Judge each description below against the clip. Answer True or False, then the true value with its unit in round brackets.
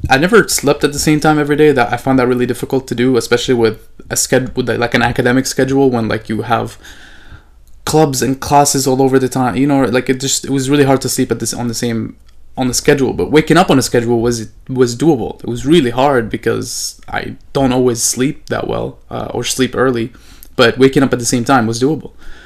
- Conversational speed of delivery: False (240 wpm)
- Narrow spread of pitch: True (2.3 semitones)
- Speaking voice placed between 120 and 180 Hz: True (130 Hz)